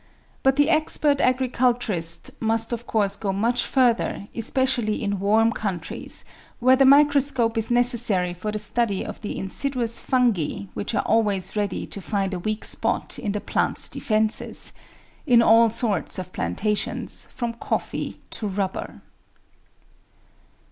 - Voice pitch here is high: Yes, high, 225 Hz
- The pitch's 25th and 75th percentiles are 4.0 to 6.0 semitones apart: No, average, 3.5 semitones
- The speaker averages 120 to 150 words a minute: Yes, average, 140 wpm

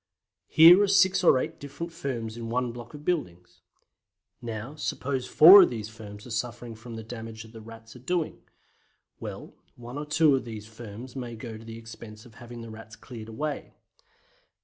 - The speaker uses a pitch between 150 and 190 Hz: No, low, 120 Hz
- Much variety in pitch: No, average, 4.0 semitones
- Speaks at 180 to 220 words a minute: Yes, average, 185 wpm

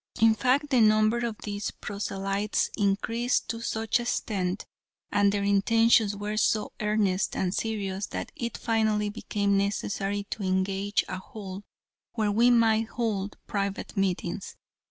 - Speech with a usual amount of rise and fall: No, narrow, 2.1 semitones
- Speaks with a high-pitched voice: Yes, high, 210 Hz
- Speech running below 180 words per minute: Yes, average, 140 wpm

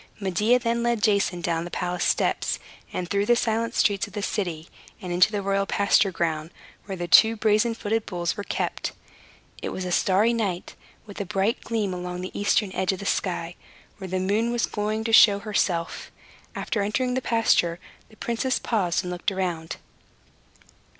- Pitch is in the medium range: No, high, 200 Hz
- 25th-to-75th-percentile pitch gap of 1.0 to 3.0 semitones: No, average, 3.7 semitones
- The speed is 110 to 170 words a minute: No, average, 185 wpm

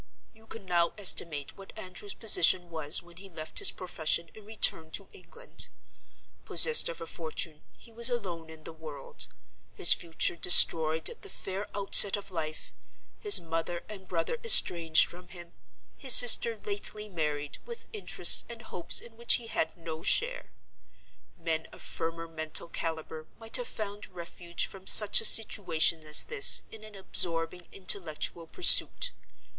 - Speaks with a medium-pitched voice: Yes, medium, 175 Hz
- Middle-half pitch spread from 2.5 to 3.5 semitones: No, average, 4.7 semitones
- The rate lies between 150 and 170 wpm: Yes, average, 155 wpm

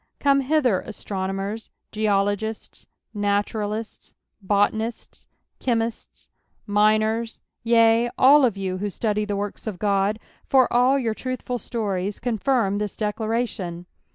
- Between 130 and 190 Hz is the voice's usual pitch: No, high, 215 Hz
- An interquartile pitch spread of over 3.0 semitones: No, narrow, 2.5 semitones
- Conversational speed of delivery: No, slow, 115 wpm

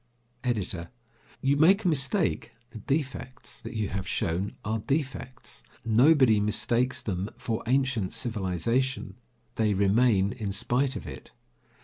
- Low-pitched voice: Yes, low, 115 Hz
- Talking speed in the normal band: No, slow, 125 wpm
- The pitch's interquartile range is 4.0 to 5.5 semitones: Yes, average, 4.6 semitones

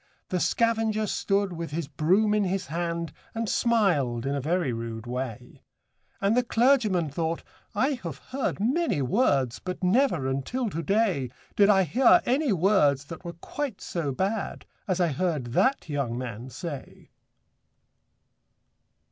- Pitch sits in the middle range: Yes, medium, 175 Hz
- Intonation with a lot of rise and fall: Yes, wide, 7.5 semitones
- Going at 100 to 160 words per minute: Yes, average, 145 wpm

